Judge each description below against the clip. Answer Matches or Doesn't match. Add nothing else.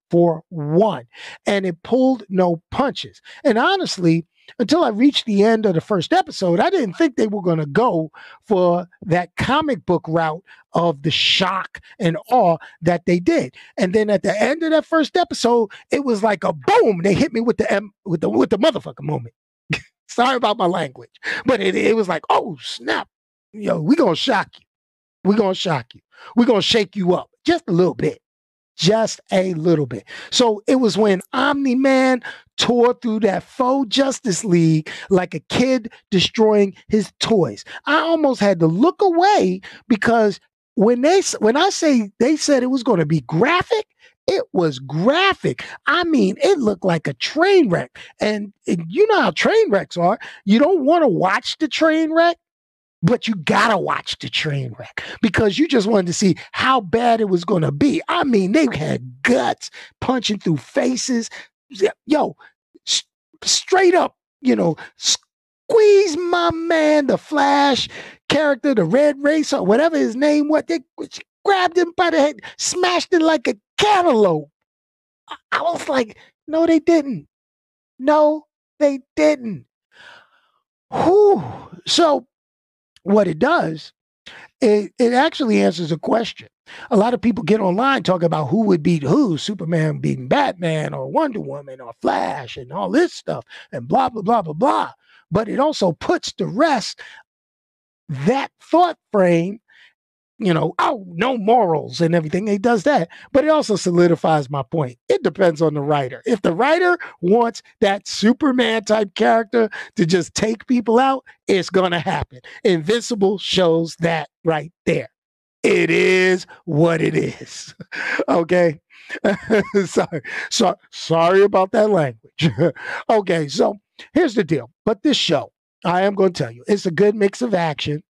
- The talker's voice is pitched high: Matches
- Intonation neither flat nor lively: Doesn't match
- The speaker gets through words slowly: Doesn't match